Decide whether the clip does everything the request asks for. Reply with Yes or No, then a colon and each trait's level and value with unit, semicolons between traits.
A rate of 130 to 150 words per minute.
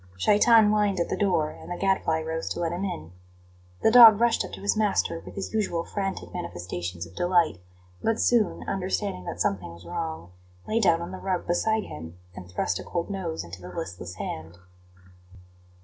No: average, 190 wpm